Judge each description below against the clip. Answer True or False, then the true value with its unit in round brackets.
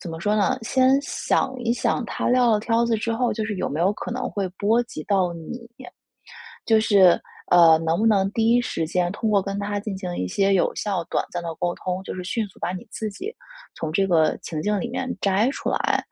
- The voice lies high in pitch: True (205 Hz)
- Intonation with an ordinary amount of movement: True (4.3 semitones)